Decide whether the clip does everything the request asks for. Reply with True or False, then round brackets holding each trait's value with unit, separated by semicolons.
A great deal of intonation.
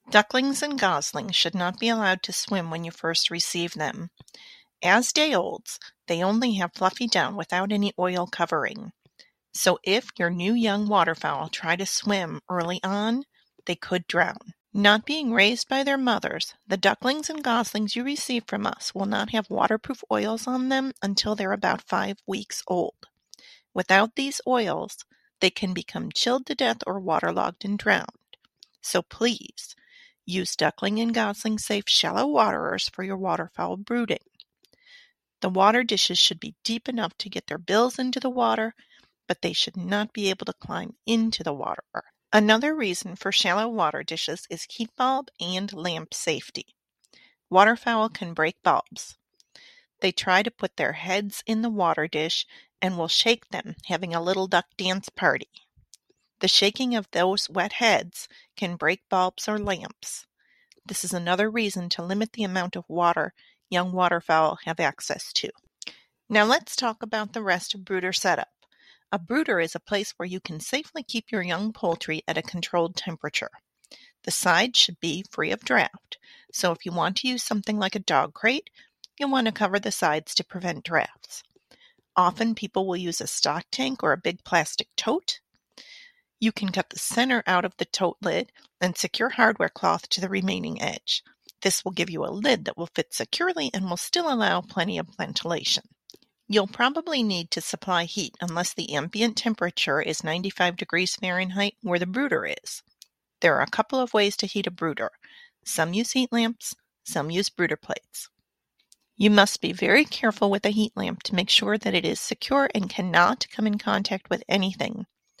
False (4.3 semitones)